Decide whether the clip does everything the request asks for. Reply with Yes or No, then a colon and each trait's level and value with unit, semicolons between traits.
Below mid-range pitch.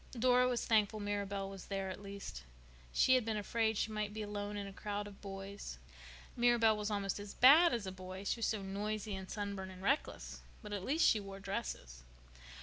No: high, 205 Hz